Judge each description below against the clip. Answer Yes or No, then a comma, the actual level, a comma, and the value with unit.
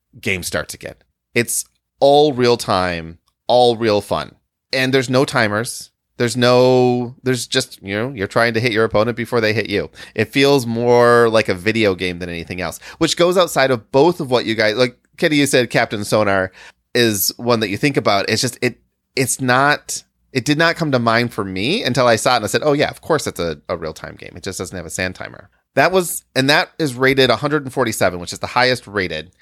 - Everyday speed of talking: No, fast, 225 wpm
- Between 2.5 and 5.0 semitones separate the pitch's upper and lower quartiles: Yes, average, 4.5 semitones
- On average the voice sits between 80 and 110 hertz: No, low, 120 Hz